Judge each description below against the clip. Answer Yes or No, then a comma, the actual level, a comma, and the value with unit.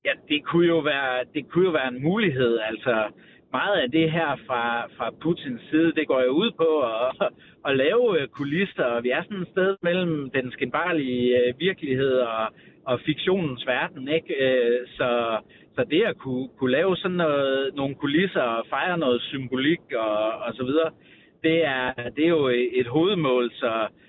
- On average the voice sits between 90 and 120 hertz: No, medium, 140 Hz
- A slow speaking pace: No, average, 170 wpm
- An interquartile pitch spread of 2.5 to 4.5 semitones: No, average, 4.9 semitones